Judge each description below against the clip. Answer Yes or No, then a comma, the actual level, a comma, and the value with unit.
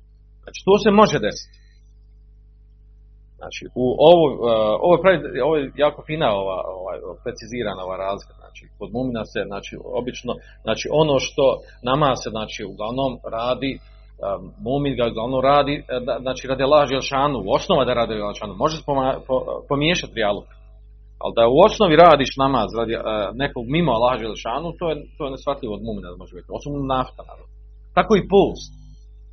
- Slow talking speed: No, average, 150 wpm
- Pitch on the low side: Yes, low, 125 Hz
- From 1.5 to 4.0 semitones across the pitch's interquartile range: No, average, 5.1 semitones